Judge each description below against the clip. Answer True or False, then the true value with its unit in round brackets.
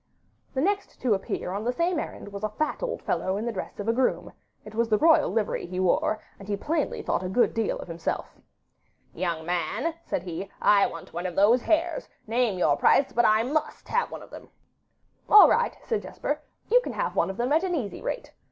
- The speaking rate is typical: False (215 wpm)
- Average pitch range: False (8.2 semitones)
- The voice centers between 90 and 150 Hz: False (225 Hz)